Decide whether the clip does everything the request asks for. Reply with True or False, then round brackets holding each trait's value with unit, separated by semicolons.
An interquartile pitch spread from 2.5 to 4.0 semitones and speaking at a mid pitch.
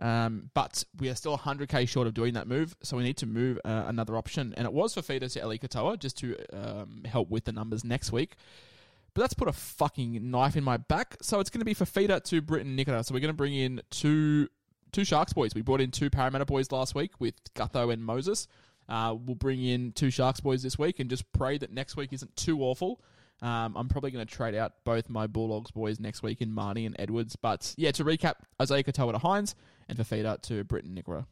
False (3.7 semitones; 125 Hz)